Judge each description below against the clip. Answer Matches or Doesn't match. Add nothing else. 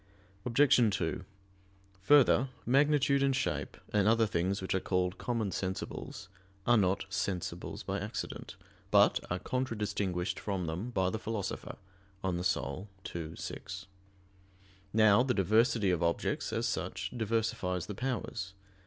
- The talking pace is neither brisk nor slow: Doesn't match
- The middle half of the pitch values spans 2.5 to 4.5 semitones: Matches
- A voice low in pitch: Matches